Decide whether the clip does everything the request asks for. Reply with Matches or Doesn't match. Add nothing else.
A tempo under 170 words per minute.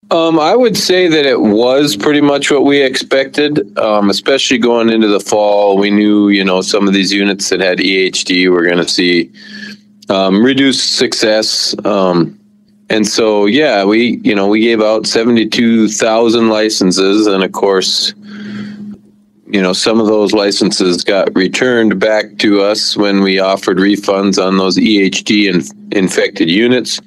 Matches